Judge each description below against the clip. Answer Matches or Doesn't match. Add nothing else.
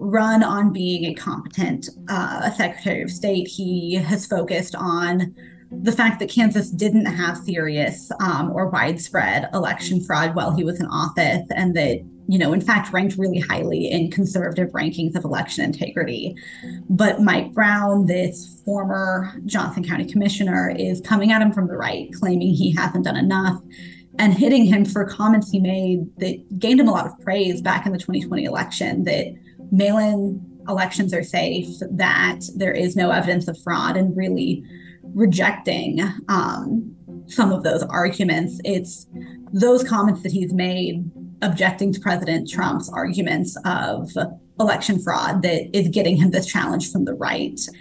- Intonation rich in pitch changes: Doesn't match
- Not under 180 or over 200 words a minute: Doesn't match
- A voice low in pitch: Doesn't match